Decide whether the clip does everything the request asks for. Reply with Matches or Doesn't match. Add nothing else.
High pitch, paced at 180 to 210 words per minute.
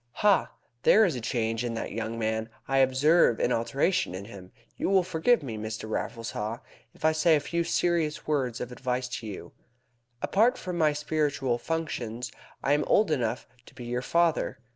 Doesn't match